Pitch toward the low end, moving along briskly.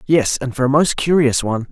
Yes: low, 130 Hz; fast, 245 wpm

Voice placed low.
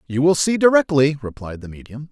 No: medium, 145 Hz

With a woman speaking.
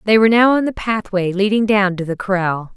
Yes: female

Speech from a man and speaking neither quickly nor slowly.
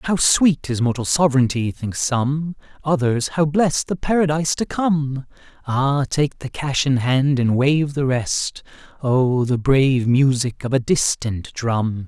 Yes: male; average, 150 wpm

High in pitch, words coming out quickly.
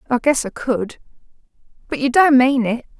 No: very high, 255 Hz; average, 160 wpm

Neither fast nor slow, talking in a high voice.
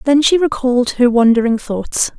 Yes: average, 165 wpm; very high, 250 Hz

